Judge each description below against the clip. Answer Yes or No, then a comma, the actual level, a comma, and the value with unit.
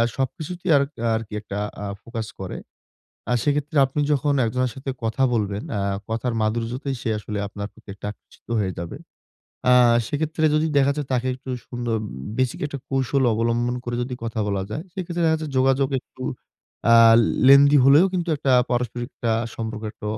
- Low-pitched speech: Yes, low, 125 Hz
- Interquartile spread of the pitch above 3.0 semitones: Yes, average, 4.0 semitones